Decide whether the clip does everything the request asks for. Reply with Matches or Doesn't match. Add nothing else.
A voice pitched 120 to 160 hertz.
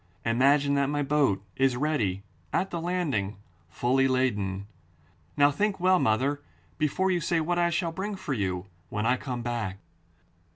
Matches